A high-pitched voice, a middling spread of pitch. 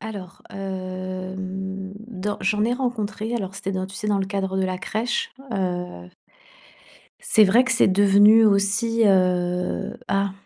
No: high, 195 Hz; narrow, 2.3 semitones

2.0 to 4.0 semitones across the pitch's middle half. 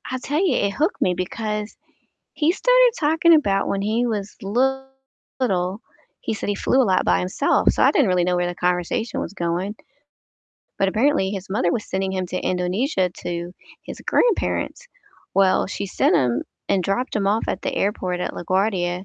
No: wide, 5.5 semitones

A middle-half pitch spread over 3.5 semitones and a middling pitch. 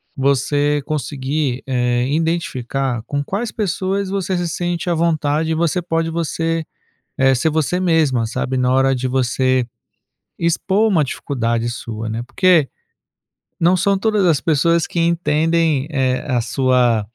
Yes: average, 4.5 semitones; medium, 150 Hz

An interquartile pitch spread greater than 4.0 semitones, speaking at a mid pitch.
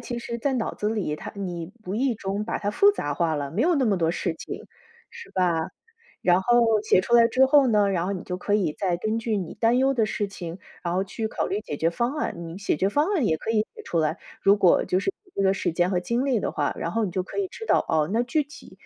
No: average, 5.0 semitones; high, 205 Hz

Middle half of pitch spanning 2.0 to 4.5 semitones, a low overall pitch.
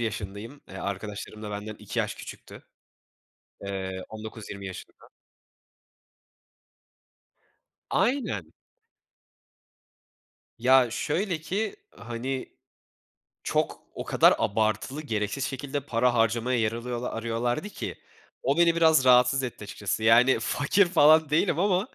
No: average, 5.3 semitones; low, 120 Hz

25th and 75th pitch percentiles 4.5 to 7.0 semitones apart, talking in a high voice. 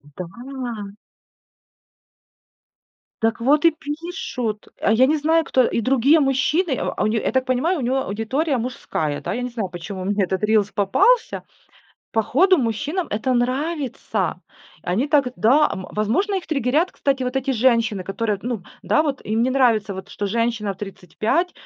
Yes: average, 5.2 semitones; high, 245 Hz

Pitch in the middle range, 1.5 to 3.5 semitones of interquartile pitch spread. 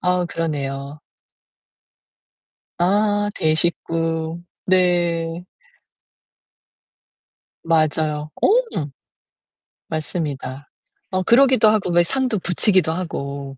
Yes: medium, 170 Hz; average, 3.2 semitones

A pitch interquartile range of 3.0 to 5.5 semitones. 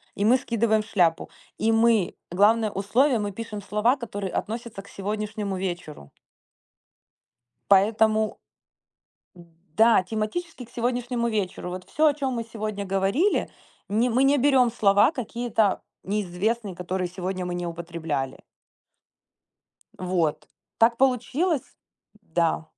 Yes: average, 3.9 semitones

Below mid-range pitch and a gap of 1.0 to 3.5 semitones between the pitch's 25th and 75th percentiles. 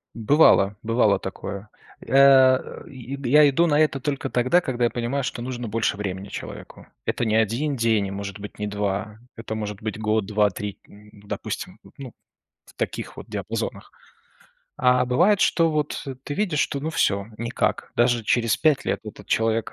No: low, 115 Hz; average, 4.7 semitones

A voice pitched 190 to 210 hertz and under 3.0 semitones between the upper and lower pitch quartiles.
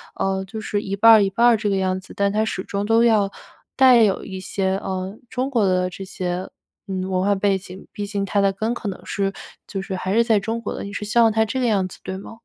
Yes: high, 200 Hz; narrow, 2.6 semitones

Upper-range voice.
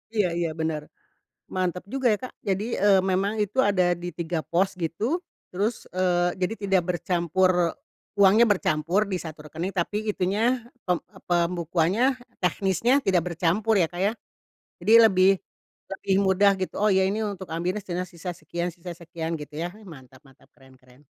No: medium, 180 Hz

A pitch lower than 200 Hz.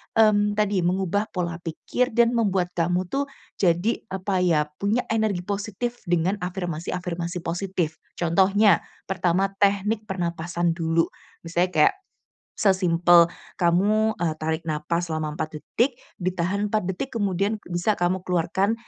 Yes: medium, 185 Hz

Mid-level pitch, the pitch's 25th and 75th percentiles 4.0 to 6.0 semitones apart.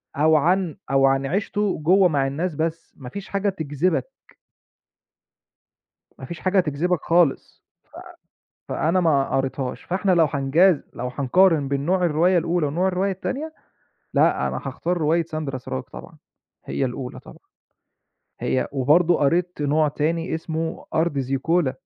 Yes: medium, 160 Hz; average, 4.3 semitones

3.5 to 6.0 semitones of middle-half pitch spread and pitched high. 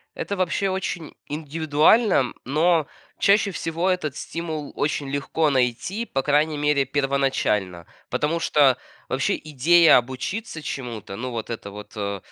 No: average, 4.5 semitones; medium, 150 Hz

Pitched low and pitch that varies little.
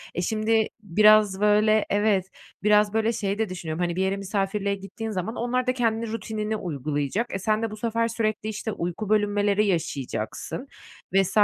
No: high, 210 Hz; narrow, 2.3 semitones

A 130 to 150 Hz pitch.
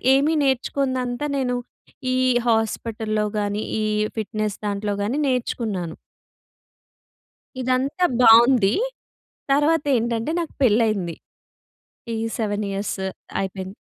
No: high, 230 Hz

